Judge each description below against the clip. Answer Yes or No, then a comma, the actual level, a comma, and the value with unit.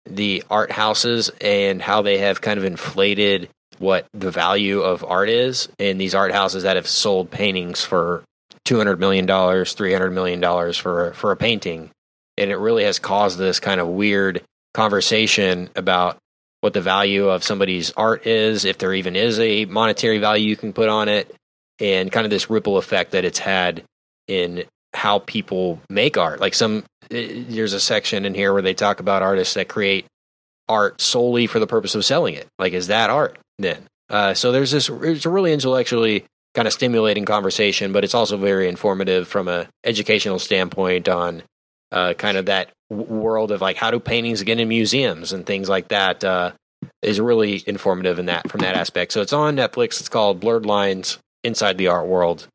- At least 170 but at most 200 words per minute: Yes, average, 190 wpm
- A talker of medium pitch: No, low, 100 Hz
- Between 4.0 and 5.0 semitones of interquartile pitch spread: No, average, 2.8 semitones